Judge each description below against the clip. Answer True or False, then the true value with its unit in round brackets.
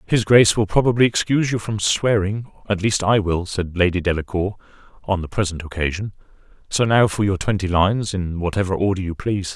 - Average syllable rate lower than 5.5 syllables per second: False (5.8 syllables/s)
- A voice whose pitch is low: True (100 Hz)